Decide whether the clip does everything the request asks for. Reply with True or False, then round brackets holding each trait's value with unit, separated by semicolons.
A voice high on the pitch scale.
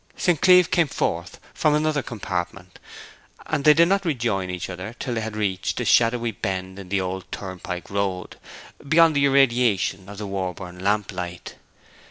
False (100 Hz)